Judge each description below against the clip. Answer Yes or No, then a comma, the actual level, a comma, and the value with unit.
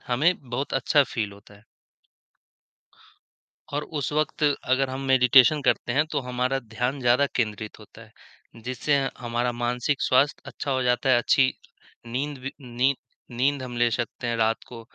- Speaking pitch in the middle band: No, low, 125 Hz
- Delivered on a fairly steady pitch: Yes, narrow, 2.3 semitones